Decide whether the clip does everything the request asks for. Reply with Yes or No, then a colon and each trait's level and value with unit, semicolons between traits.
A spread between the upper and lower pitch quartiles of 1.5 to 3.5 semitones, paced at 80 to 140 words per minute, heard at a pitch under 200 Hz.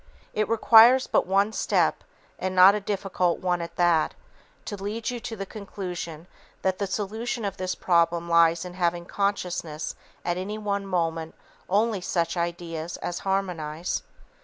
No: average, 2.9 semitones; average, 160 wpm; medium, 185 Hz